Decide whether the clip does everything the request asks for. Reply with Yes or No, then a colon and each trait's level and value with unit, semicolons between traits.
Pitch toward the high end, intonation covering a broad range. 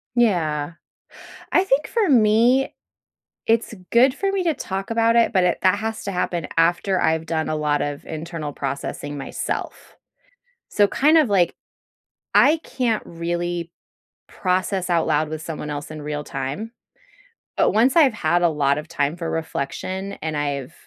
No: medium, 175 Hz; wide, 6.7 semitones